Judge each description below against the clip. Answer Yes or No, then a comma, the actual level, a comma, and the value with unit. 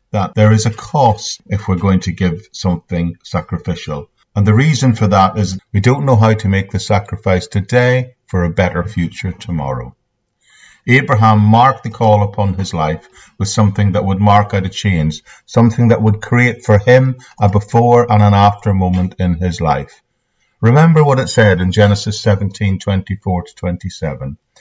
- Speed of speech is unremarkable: Yes, average, 175 wpm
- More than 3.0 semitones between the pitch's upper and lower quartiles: Yes, average, 3.4 semitones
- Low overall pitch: Yes, low, 100 Hz